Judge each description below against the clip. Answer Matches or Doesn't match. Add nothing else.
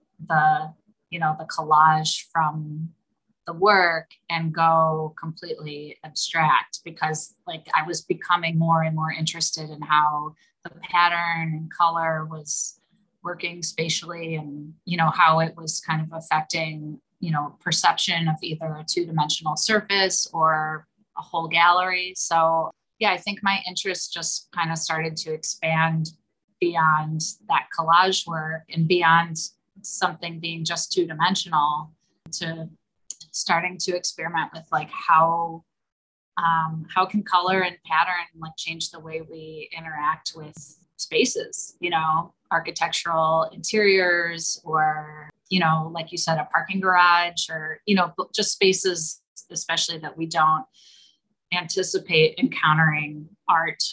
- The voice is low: Doesn't match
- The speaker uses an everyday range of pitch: Doesn't match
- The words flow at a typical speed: Doesn't match